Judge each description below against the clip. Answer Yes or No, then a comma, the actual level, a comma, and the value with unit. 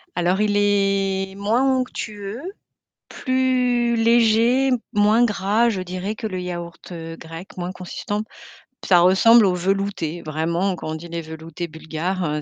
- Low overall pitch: No, high, 195 Hz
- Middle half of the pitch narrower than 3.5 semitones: No, average, 4.2 semitones